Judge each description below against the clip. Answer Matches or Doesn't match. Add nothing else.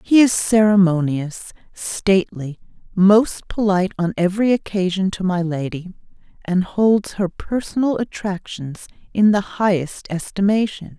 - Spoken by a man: Doesn't match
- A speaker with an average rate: Doesn't match